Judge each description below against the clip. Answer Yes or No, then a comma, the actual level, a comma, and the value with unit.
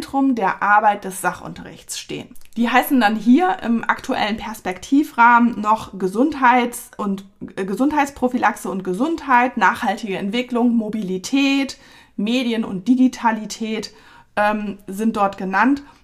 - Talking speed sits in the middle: No, slow, 110 wpm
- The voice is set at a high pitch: Yes, high, 230 Hz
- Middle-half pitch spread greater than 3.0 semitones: Yes, average, 4.1 semitones